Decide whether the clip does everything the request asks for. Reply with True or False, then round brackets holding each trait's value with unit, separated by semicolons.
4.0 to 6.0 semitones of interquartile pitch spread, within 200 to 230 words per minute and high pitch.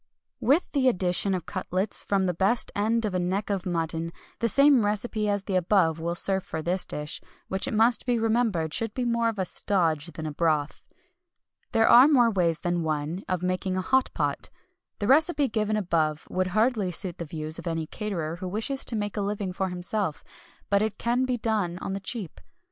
True (4.5 semitones; 205 wpm; 195 Hz)